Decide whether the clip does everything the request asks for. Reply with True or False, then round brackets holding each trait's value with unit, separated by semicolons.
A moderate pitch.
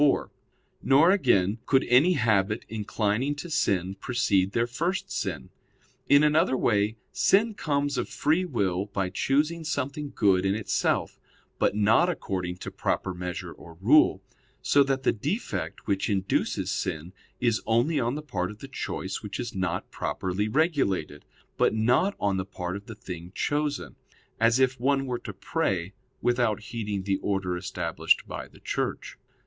False (110 Hz)